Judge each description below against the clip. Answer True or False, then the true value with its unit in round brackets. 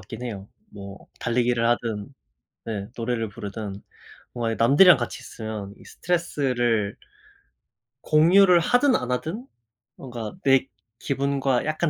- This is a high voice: False (120 Hz)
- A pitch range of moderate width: True (4.6 semitones)